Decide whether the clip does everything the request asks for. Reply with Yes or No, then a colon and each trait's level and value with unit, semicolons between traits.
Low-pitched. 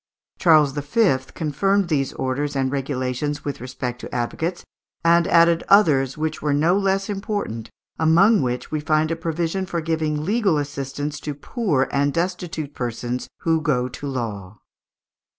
No: medium, 150 Hz